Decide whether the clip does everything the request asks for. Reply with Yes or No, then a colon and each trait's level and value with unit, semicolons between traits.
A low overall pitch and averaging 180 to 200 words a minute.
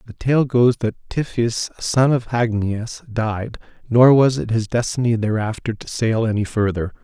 No: low, 115 Hz; average, 160 wpm